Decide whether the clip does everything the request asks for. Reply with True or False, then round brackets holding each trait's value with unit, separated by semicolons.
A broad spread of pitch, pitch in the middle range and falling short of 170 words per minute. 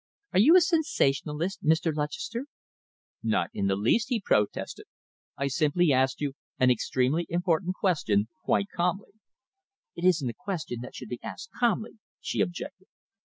True (6.7 semitones; 165 Hz; 150 wpm)